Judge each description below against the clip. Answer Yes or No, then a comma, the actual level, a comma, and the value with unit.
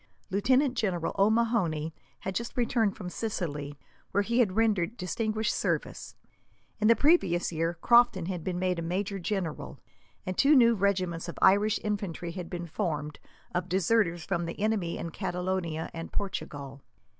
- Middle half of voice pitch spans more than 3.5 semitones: Yes, average, 4.3 semitones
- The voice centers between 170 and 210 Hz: Yes, medium, 185 Hz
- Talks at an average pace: Yes, average, 155 wpm